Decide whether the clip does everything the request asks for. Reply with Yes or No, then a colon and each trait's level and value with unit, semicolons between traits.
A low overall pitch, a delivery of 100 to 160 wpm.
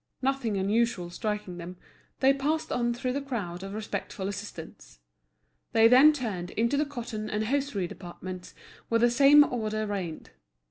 No: high, 220 Hz; average, 150 wpm